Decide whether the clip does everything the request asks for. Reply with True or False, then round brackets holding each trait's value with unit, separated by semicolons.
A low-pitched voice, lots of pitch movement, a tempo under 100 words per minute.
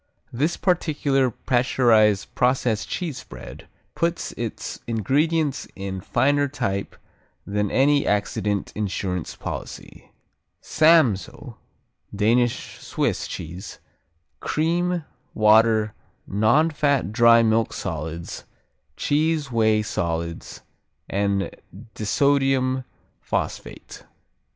True (115 Hz; 5.7 semitones; 85 wpm)